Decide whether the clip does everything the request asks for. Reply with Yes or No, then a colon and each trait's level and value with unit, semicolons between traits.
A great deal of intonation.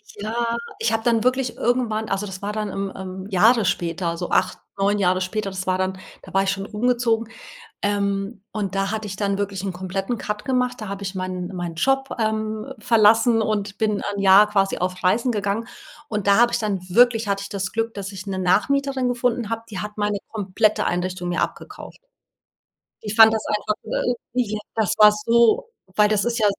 No: average, 2.7 semitones